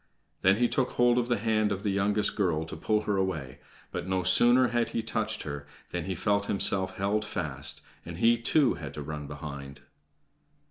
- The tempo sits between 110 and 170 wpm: No, average, 195 wpm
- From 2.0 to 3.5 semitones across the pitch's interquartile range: No, average, 4.7 semitones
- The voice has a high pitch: No, low, 100 Hz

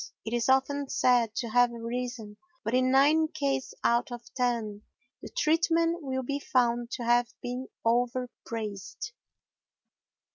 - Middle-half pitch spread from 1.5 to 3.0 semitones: Yes, narrow, 2.4 semitones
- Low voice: No, high, 245 Hz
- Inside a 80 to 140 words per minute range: Yes, slow, 135 wpm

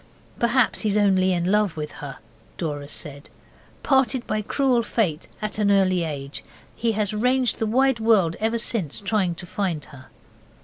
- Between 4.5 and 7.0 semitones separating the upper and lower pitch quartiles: Yes, average, 5.3 semitones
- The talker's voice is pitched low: No, high, 205 Hz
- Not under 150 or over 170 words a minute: Yes, average, 165 wpm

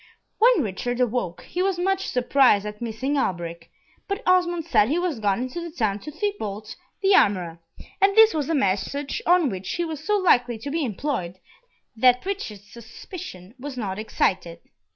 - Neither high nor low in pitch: No, very high, 255 Hz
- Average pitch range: No, wide, 8.9 semitones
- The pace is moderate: Yes, average, 175 wpm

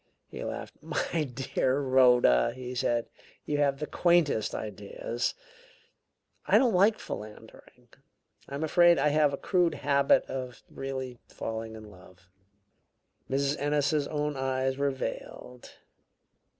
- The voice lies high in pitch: No, low, 135 Hz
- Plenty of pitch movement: No, average, 3.2 semitones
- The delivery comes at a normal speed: No, slow, 125 wpm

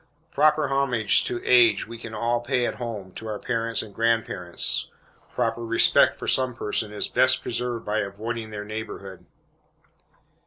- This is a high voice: No, low, 115 Hz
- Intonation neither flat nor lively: No, narrow, 2.3 semitones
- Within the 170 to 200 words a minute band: No, average, 155 wpm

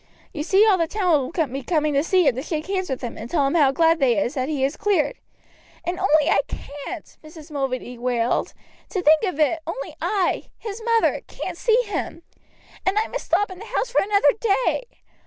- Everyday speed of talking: No, fast, 215 wpm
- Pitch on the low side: No, very high, 325 Hz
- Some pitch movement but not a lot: No, wide, 5.8 semitones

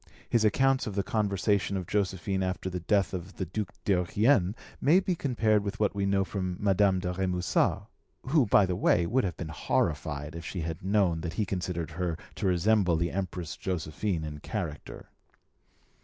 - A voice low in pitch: Yes, very low, 95 Hz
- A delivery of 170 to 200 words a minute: Yes, average, 180 wpm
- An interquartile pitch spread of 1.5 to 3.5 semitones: Yes, average, 3.0 semitones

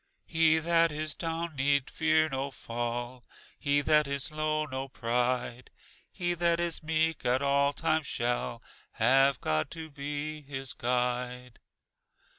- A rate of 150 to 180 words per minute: No, slow, 135 wpm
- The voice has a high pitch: No, medium, 140 Hz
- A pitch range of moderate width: Yes, average, 3.9 semitones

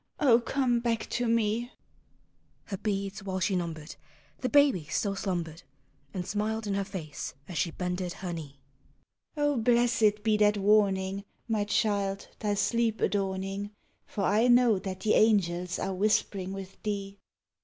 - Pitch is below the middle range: No, high, 200 Hz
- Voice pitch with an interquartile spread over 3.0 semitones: No, average, 2.7 semitones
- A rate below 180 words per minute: Yes, average, 160 wpm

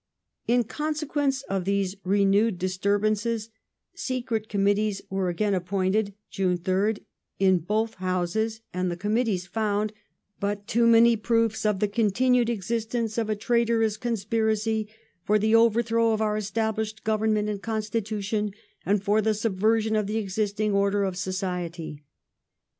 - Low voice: No, high, 215 Hz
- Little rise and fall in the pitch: Yes, narrow, 2.2 semitones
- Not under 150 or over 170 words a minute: No, average, 140 wpm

